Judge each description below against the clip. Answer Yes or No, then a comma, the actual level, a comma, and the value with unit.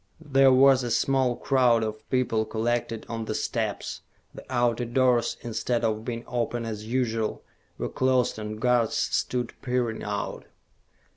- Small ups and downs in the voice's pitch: Yes, narrow, 2.2 semitones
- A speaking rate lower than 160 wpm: Yes, average, 145 wpm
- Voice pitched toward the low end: Yes, low, 120 Hz